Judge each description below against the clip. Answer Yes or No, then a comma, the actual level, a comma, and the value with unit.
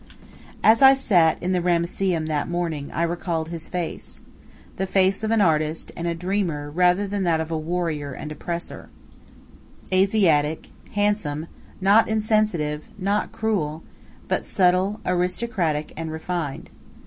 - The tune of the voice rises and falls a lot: No, average, 3.6 semitones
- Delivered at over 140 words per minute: No, slow, 135 wpm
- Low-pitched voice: No, medium, 175 Hz